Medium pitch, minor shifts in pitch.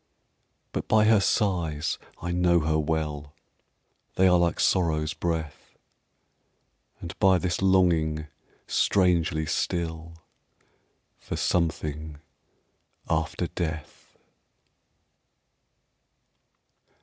No: very low, 85 Hz; narrow, 2.3 semitones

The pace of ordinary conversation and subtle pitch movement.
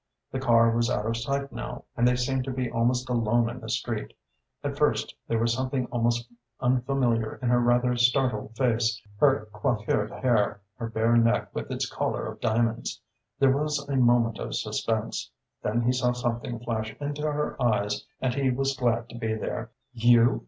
Yes: average, 180 wpm; narrow, 2.0 semitones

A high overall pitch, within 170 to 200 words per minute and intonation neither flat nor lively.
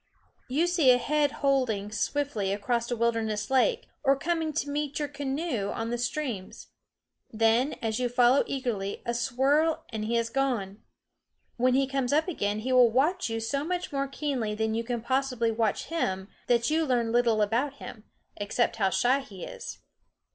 Yes: high, 245 Hz; average, 175 wpm; average, 3.8 semitones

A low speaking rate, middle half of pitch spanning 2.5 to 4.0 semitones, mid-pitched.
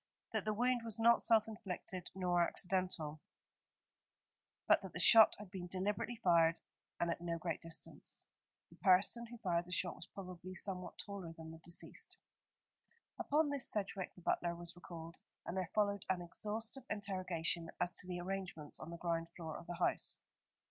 No: average, 170 wpm; average, 3.2 semitones; medium, 180 Hz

